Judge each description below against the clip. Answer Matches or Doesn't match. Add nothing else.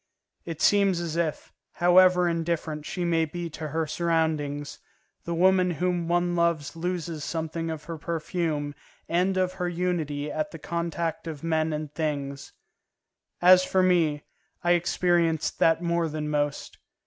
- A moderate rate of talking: Matches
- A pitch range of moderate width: Doesn't match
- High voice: Doesn't match